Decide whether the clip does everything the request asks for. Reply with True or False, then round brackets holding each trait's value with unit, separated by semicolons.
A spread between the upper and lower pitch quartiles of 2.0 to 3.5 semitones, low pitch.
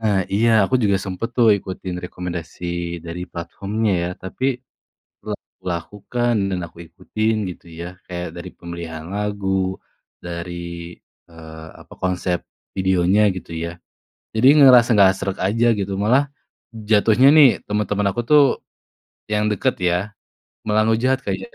False (3.9 semitones; 100 Hz)